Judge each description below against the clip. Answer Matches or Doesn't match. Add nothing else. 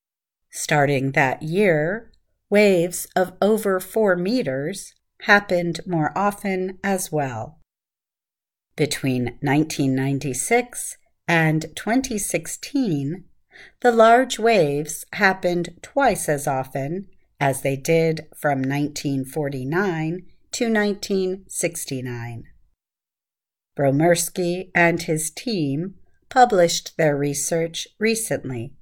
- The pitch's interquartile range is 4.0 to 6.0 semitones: Matches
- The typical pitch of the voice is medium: Matches